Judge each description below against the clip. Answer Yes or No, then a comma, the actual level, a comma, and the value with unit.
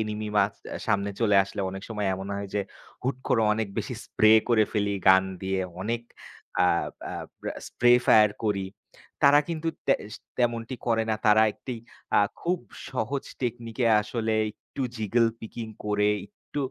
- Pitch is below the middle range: Yes, low, 110 Hz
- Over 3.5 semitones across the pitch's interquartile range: No, narrow, 2.6 semitones